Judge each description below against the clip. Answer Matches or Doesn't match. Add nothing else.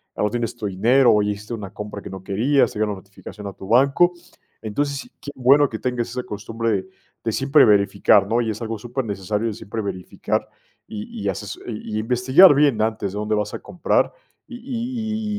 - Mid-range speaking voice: Doesn't match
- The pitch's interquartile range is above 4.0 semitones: Matches